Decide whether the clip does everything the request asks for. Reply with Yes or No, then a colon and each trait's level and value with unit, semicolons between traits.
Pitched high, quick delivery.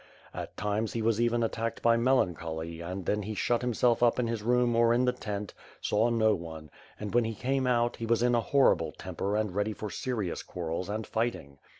No: low, 110 Hz; fast, 220 wpm